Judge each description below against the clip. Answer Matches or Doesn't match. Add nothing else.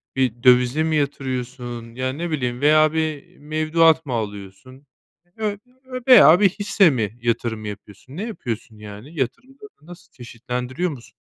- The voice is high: Doesn't match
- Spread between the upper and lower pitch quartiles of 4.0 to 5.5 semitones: Matches